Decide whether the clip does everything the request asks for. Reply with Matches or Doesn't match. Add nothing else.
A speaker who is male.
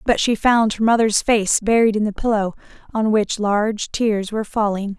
Doesn't match